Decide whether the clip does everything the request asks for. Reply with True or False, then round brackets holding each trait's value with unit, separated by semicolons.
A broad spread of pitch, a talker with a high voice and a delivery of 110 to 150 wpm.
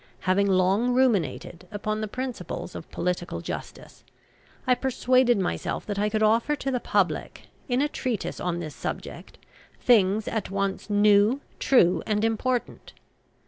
False (4.4 semitones; 215 Hz; 140 wpm)